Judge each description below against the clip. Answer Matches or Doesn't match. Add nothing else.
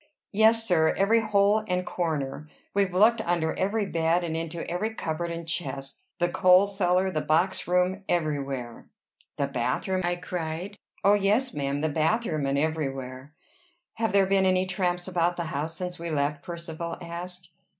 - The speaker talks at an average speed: Matches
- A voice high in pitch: Doesn't match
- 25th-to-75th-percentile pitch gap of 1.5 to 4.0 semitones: Matches